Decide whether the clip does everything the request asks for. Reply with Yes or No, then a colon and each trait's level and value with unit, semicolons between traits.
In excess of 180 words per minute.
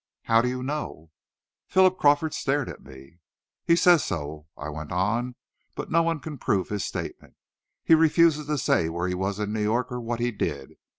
Yes: average, 195 wpm